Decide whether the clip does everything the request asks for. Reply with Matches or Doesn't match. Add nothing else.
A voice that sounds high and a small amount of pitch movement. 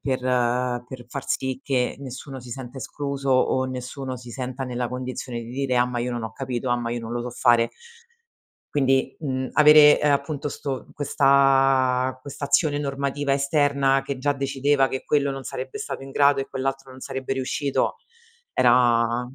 Doesn't match